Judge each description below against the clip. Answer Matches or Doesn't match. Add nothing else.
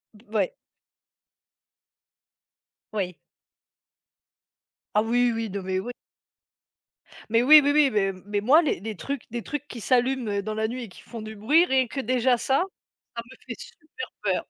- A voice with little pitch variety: Doesn't match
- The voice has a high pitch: Matches